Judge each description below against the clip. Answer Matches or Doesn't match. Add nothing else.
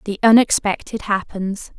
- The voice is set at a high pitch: Matches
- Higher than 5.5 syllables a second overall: Doesn't match